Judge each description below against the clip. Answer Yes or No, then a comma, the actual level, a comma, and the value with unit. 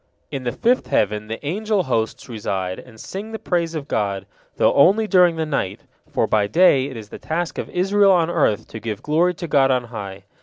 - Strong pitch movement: Yes, wide, 8.6 semitones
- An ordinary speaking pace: No, fast, 215 wpm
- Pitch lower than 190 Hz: Yes, medium, 140 Hz